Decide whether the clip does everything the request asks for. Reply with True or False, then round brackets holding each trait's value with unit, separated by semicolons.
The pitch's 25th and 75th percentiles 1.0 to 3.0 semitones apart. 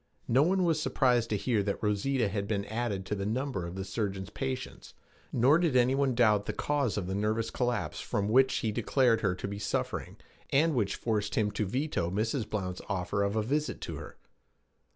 False (4.4 semitones)